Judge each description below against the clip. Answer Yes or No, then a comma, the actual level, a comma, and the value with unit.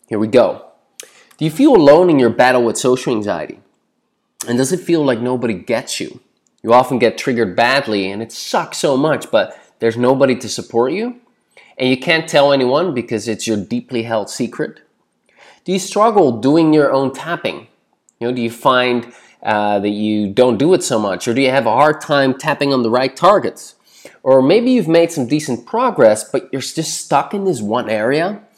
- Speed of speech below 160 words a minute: No, average, 200 wpm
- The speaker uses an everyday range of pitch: Yes, average, 4.8 semitones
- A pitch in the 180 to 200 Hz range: No, low, 130 Hz